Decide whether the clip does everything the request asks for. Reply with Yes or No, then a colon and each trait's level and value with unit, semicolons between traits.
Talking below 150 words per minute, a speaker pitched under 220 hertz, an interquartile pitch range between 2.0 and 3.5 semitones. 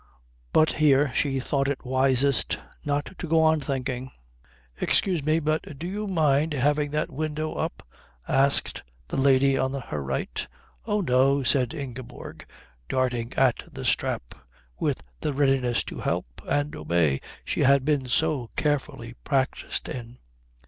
Yes: average, 140 wpm; medium, 140 Hz; average, 2.7 semitones